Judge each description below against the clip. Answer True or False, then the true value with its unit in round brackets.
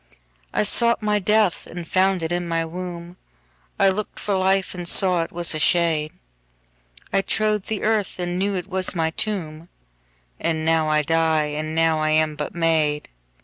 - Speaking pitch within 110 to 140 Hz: False (170 Hz)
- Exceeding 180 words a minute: False (165 wpm)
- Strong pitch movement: False (3.4 semitones)